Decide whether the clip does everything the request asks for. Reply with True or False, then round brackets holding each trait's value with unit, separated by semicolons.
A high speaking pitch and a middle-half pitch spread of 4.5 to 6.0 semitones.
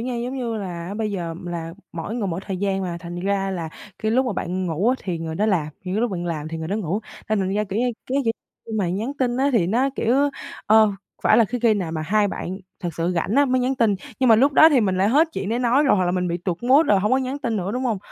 True (205 Hz; 5.2 semitones)